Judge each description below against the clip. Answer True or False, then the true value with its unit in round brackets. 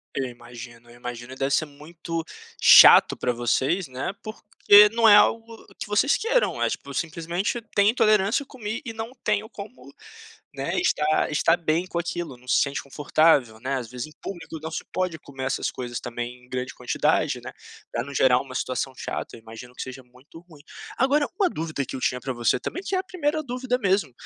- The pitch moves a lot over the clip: True (8.6 semitones)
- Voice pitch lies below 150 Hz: False (155 Hz)